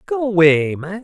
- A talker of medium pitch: Yes, medium, 175 Hz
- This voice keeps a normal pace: Yes, average, 175 wpm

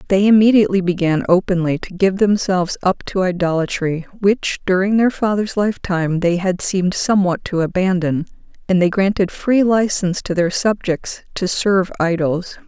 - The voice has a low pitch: No, medium, 185 Hz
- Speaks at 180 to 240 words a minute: No, average, 150 wpm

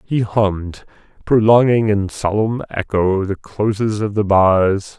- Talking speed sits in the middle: No, slow, 130 wpm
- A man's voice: Yes, male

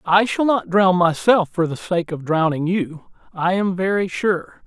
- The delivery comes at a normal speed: Yes, average, 195 wpm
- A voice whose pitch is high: No, medium, 180 Hz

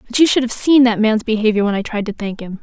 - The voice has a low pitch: No, high, 225 Hz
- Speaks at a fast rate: Yes, fast, 320 wpm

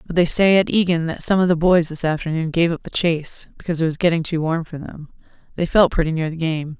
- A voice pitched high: No, medium, 165 Hz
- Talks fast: Yes, fast, 265 wpm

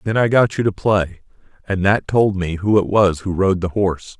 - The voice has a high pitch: No, low, 100 Hz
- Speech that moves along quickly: Yes, fast, 245 wpm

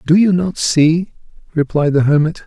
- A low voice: No, medium, 160 Hz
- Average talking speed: Yes, average, 170 wpm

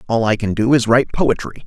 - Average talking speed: No, fast, 255 wpm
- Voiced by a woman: No, male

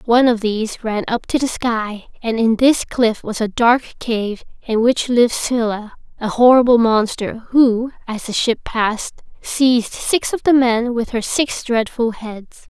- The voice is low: No, high, 235 Hz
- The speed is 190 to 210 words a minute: No, average, 180 wpm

